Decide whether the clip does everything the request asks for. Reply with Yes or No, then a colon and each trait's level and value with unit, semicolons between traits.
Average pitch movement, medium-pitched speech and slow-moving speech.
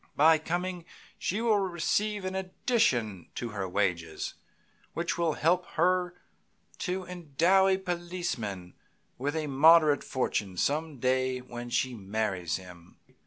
No: wide, 8.1 semitones; medium, 155 Hz; slow, 125 wpm